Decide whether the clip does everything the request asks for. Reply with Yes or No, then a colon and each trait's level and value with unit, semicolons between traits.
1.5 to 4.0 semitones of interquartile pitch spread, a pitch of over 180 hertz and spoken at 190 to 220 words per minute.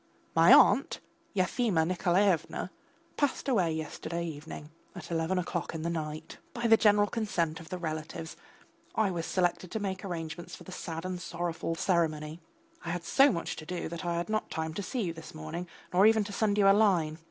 No: average, 3.5 semitones; medium, 175 Hz; average, 200 wpm